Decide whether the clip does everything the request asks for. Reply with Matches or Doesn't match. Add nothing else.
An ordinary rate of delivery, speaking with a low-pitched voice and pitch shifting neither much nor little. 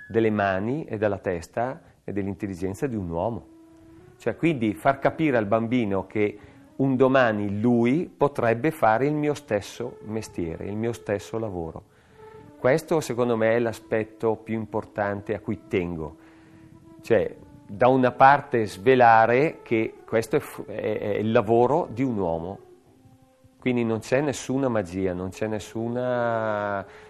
Matches